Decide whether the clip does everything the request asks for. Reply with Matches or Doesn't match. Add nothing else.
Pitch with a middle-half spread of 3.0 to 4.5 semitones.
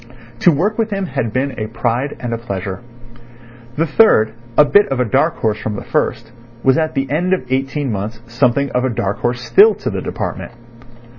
Doesn't match